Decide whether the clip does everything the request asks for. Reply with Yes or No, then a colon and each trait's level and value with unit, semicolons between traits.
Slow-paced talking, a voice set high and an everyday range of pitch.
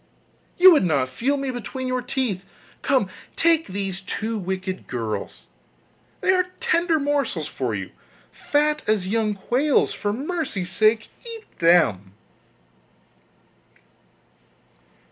No: slow, 115 wpm; high, 225 Hz; wide, 7.8 semitones